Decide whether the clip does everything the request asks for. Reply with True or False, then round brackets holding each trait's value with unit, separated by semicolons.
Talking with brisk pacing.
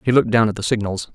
True (315 wpm)